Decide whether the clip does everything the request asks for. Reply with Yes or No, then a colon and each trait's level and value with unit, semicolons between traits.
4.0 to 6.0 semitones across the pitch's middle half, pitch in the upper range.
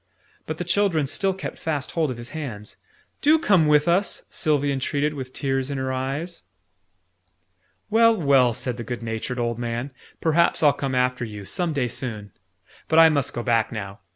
No: average, 4.9 semitones; medium, 140 Hz